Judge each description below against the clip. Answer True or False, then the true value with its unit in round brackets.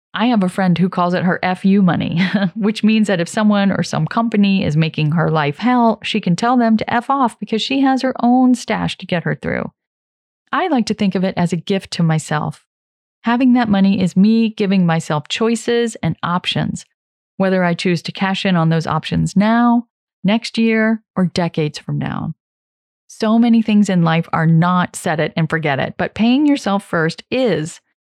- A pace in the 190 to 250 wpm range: True (200 wpm)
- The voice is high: True (195 Hz)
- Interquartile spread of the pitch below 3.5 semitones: False (4.7 semitones)